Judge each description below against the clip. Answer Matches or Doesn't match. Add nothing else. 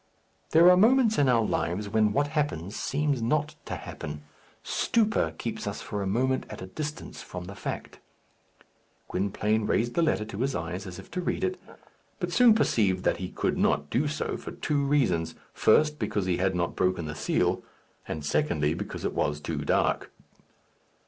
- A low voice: Matches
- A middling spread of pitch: Doesn't match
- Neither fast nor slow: Matches